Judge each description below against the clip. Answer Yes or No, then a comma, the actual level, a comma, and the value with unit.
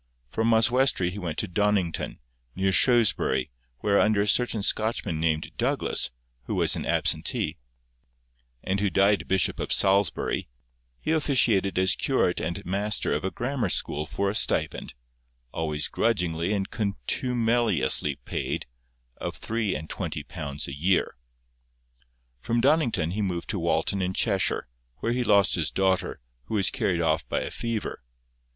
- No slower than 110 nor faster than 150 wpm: Yes, average, 145 wpm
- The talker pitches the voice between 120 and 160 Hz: No, very low, 95 Hz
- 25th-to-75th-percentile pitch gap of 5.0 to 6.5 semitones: Yes, average, 5.3 semitones